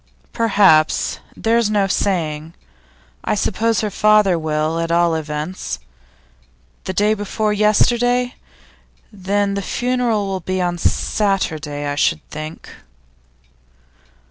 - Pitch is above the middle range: Yes, high, 195 Hz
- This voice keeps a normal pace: No, slow, 110 wpm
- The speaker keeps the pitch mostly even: No, average, 4.7 semitones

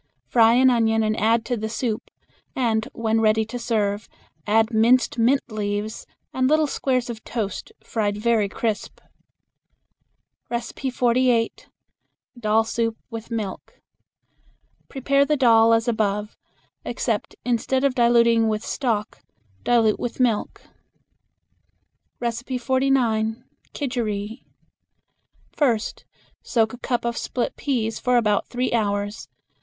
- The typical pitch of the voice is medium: No, high, 230 Hz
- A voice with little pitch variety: Yes, narrow, 2.2 semitones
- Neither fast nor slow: No, slow, 115 wpm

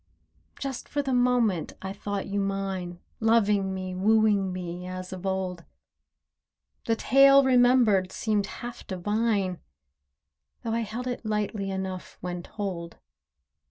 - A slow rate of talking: Yes, slow, 125 wpm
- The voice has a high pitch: Yes, high, 200 Hz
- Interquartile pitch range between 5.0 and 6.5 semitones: No, average, 3.5 semitones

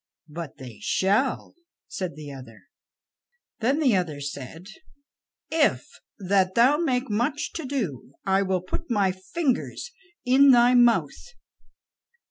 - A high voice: Yes, high, 205 Hz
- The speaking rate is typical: No, slow, 120 wpm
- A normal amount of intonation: No, wide, 7.3 semitones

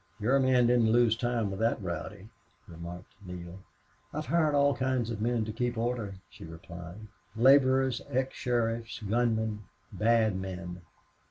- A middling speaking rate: Yes, average, 145 wpm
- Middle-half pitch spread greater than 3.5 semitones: Yes, average, 4.1 semitones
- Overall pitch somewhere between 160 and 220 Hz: No, low, 115 Hz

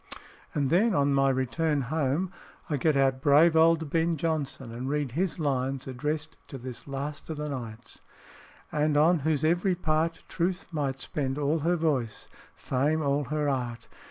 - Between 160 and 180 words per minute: Yes, average, 170 wpm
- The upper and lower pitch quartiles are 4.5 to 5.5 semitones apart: No, average, 3.0 semitones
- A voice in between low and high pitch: Yes, medium, 145 Hz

